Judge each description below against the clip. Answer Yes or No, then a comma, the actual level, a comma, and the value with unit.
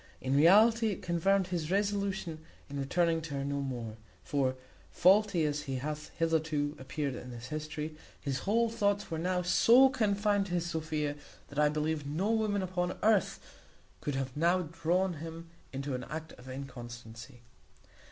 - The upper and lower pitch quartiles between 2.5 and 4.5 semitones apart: No, average, 5.0 semitones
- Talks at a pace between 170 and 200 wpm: No, average, 160 wpm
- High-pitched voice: No, medium, 160 Hz